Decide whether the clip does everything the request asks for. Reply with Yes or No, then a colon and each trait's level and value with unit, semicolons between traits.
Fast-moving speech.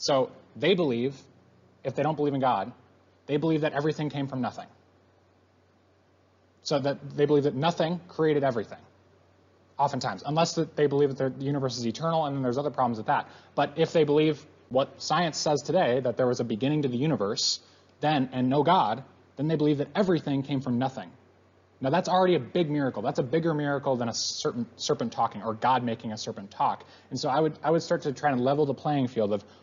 Yes: fast, 215 wpm